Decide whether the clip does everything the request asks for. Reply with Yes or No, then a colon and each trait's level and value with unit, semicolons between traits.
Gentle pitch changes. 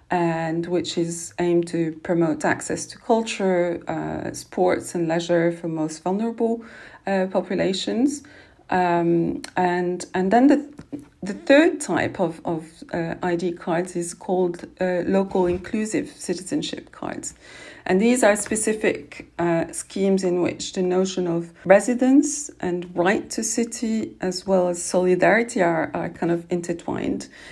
No: average, 3.4 semitones